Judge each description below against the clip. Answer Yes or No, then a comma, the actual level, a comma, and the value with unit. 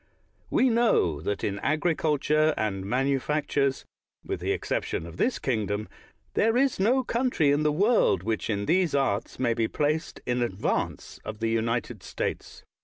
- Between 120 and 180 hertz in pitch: Yes, low, 135 Hz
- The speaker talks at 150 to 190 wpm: Yes, average, 155 wpm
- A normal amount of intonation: No, wide, 6.8 semitones